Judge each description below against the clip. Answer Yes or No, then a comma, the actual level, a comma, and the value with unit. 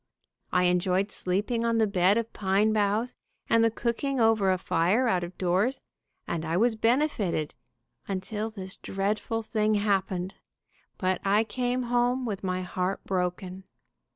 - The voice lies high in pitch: Yes, high, 205 Hz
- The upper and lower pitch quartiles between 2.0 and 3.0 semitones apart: No, average, 3.6 semitones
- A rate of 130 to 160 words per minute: Yes, average, 150 wpm